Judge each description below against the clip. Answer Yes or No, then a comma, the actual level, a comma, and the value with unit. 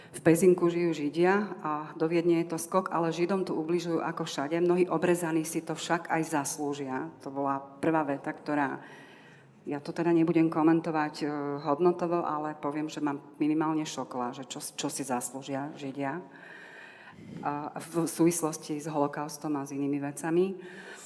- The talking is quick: No, average, 155 wpm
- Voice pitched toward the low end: No, medium, 155 Hz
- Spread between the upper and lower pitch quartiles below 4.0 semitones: Yes, narrow, 2.6 semitones